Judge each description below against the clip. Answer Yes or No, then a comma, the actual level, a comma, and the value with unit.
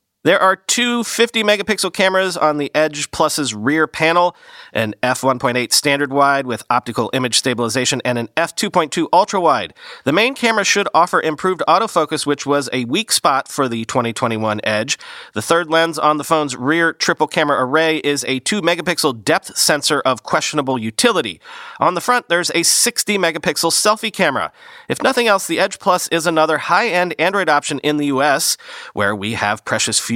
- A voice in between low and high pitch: Yes, medium, 155 Hz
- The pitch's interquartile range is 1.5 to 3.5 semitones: No, wide, 5.5 semitones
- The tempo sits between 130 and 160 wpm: No, average, 175 wpm